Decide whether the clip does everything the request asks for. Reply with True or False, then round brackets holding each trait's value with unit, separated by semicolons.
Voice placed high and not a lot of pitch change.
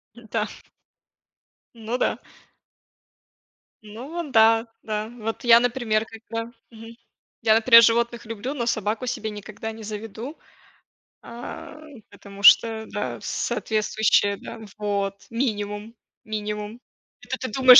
True (225 Hz; 1.9 semitones)